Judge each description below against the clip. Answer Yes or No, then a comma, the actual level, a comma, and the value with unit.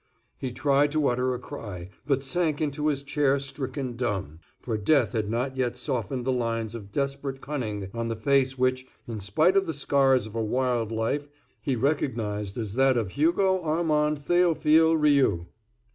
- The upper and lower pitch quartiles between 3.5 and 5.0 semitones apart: Yes, average, 4.3 semitones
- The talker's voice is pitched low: Yes, low, 130 Hz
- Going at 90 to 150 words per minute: No, average, 175 wpm